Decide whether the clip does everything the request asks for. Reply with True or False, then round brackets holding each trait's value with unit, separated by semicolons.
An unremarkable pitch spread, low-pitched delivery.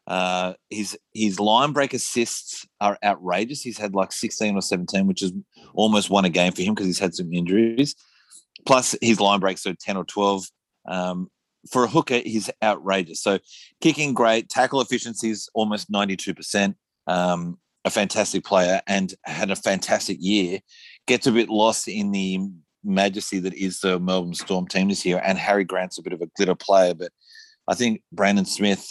True (3.0 semitones; 100 Hz)